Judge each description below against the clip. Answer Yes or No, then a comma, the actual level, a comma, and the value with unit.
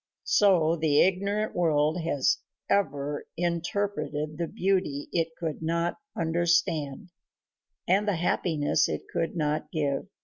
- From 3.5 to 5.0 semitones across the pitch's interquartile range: No, average, 2.8 semitones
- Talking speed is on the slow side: Yes, slow, 115 wpm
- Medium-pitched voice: Yes, medium, 165 Hz